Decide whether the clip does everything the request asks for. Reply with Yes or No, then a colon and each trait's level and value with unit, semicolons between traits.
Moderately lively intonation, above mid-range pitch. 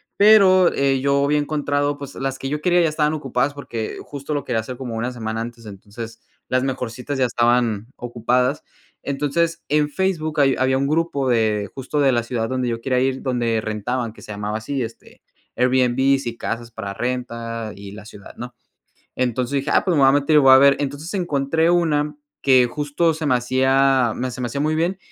No: average, 3.5 semitones; low, 130 Hz